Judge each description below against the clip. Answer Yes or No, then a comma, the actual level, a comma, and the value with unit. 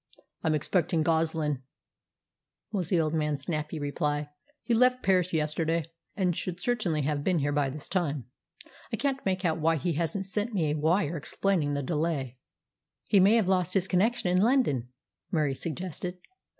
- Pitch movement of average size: Yes, average, 3.8 semitones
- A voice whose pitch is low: No, medium, 165 Hz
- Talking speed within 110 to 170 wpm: Yes, average, 165 wpm